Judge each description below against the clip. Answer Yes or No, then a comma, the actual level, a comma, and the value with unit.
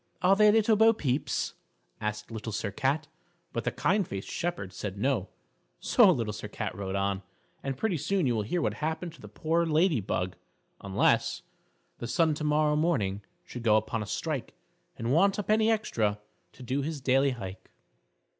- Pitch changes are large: Yes, wide, 7.9 semitones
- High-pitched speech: No, low, 135 Hz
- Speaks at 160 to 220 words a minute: Yes, average, 180 wpm